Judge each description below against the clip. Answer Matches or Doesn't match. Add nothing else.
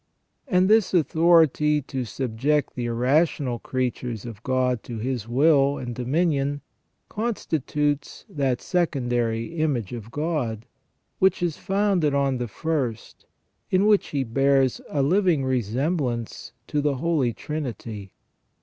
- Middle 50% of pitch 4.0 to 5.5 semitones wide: Matches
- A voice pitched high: Doesn't match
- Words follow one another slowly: Matches